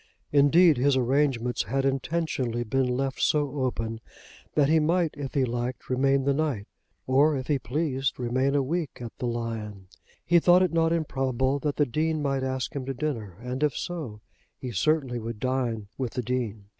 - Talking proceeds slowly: No, average, 180 wpm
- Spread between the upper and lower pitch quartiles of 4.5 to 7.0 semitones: No, average, 3.3 semitones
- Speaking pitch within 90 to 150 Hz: Yes, low, 135 Hz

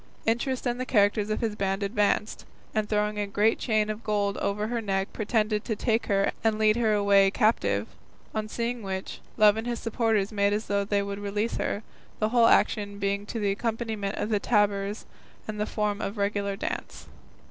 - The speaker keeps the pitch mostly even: Yes, narrow, 1.7 semitones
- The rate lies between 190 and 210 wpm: Yes, average, 200 wpm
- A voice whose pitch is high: Yes, high, 210 Hz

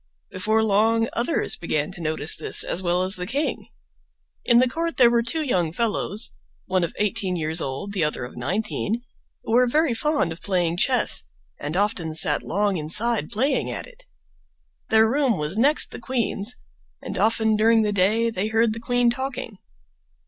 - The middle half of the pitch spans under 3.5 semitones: No, average, 4.8 semitones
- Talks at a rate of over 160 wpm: Yes, average, 180 wpm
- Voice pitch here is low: No, high, 215 Hz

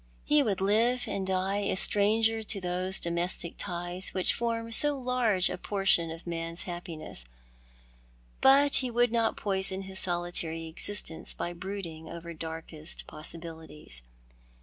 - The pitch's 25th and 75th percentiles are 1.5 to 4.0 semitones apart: No, average, 4.4 semitones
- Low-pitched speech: No, medium, 185 Hz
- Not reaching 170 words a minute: Yes, average, 140 wpm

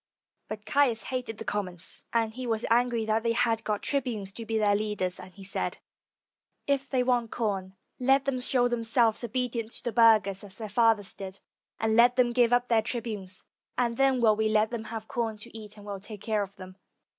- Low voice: No, high, 225 Hz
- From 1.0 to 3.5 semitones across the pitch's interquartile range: Yes, narrow, 2.6 semitones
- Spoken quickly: Yes, fast, 215 wpm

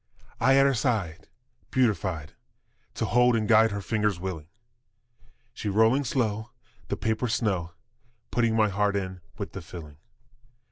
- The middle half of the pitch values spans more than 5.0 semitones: No, average, 3.6 semitones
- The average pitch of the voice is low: Yes, low, 105 Hz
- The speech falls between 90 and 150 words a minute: Yes, average, 140 wpm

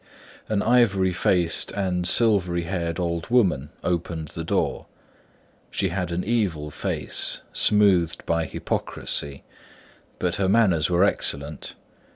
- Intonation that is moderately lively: Yes, average, 3.2 semitones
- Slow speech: Yes, slow, 120 wpm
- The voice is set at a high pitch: No, very low, 90 Hz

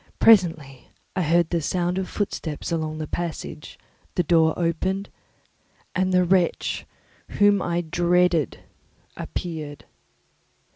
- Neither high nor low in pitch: Yes, medium, 175 Hz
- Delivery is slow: Yes, slow, 110 wpm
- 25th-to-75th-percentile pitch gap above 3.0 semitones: No, narrow, 2.4 semitones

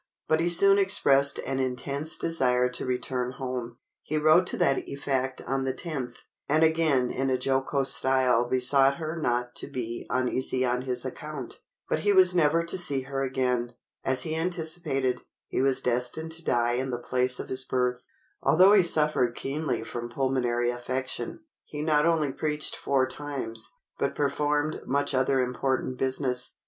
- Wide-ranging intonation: No, average, 3.4 semitones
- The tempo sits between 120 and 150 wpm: No, average, 165 wpm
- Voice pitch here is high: No, low, 135 Hz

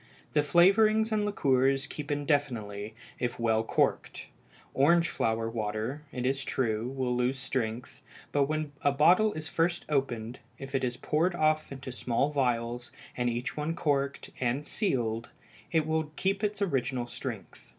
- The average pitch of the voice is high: No, low, 135 Hz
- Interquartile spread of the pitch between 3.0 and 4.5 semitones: Yes, average, 4.2 semitones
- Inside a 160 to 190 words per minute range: No, average, 150 wpm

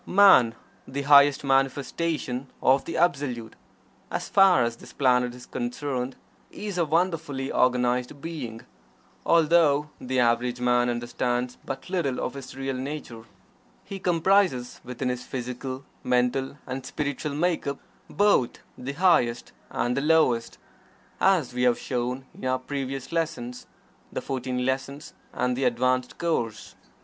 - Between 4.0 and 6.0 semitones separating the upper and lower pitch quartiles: No, average, 3.1 semitones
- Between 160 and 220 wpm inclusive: No, slow, 135 wpm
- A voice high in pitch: No, low, 130 Hz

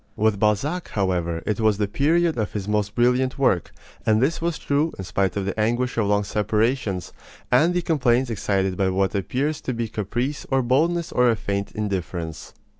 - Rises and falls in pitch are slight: No, average, 4.8 semitones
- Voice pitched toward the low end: Yes, low, 110 Hz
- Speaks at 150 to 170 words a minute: No, average, 190 wpm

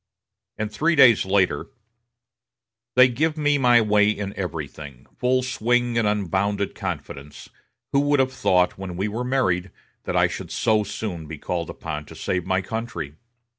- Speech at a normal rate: Yes, average, 160 wpm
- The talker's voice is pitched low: Yes, low, 105 Hz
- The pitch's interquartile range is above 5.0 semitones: Yes, wide, 5.4 semitones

